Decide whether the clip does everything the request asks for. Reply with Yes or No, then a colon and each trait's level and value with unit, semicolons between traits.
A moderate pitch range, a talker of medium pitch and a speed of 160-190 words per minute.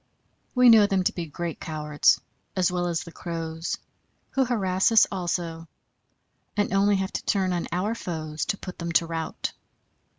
Yes: average, 3.1 semitones; medium, 180 Hz; average, 170 wpm